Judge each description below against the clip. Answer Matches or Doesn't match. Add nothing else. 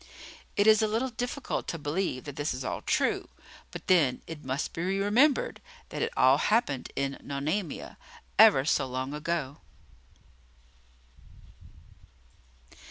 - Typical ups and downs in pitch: Doesn't match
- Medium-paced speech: Doesn't match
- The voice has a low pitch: Doesn't match